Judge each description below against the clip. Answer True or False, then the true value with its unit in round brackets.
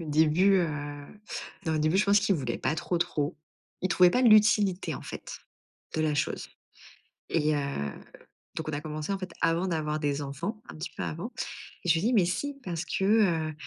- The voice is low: False (170 Hz)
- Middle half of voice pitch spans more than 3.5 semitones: True (3.9 semitones)